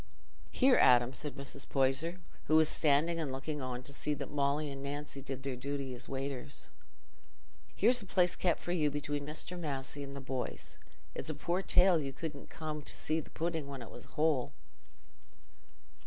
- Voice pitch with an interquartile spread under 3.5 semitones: Yes, average, 2.8 semitones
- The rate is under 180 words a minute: No, average, 185 wpm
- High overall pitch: No, medium, 145 Hz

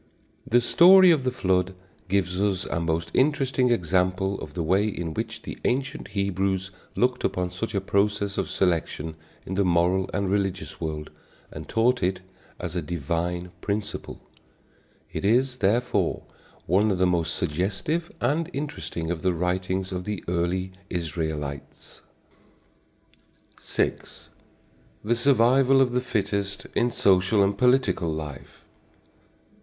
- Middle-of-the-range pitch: No, very low, 95 Hz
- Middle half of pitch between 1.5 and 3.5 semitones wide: No, average, 4.8 semitones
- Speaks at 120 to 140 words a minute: Yes, slow, 135 wpm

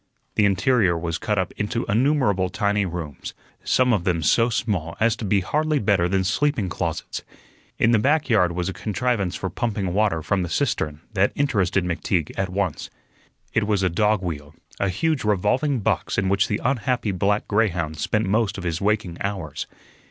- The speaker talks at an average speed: Yes, average, 180 wpm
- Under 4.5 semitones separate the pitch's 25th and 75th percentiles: Yes, average, 3.7 semitones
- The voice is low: Yes, low, 100 Hz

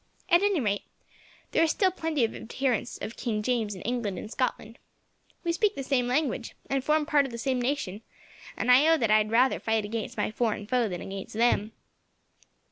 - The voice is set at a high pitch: Yes, high, 245 Hz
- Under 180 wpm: No, fast, 205 wpm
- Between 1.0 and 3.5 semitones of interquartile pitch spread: No, average, 4.6 semitones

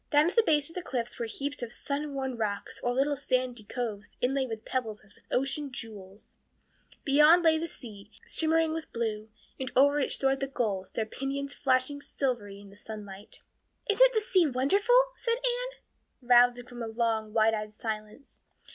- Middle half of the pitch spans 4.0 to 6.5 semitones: Yes, average, 4.9 semitones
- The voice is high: Yes, very high, 255 Hz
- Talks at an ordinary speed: Yes, average, 180 wpm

